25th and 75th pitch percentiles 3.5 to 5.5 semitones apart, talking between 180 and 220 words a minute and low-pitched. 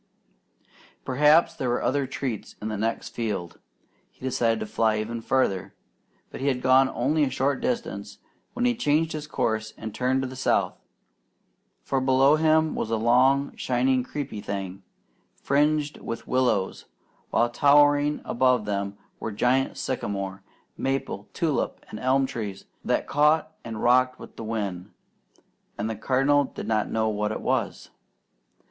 No: average, 4.4 semitones; average, 155 wpm; low, 130 Hz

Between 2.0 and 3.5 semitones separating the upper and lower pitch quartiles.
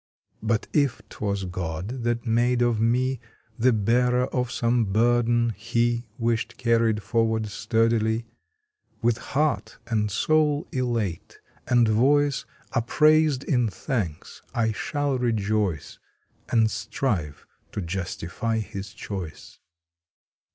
Yes: narrow, 2.6 semitones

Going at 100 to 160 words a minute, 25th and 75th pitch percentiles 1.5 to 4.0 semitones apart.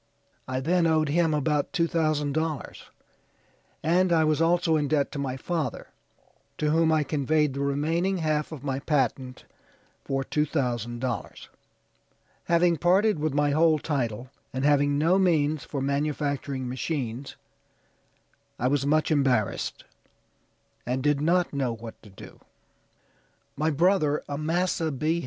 Yes: average, 140 wpm; average, 3.0 semitones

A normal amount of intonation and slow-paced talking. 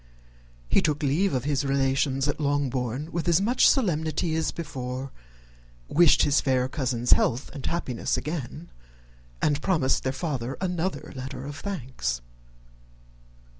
Yes: average, 3.7 semitones; slow, 130 wpm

